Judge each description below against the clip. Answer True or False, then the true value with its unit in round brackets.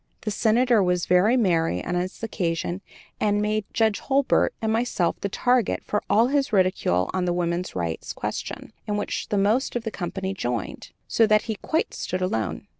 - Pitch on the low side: False (200 Hz)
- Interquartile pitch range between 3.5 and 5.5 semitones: True (4.0 semitones)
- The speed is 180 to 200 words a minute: True (185 wpm)